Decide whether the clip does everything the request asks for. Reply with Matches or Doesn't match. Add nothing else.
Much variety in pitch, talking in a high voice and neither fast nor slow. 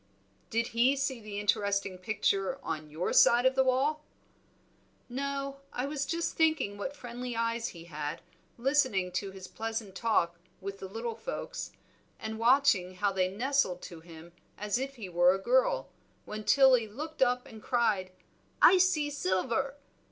Matches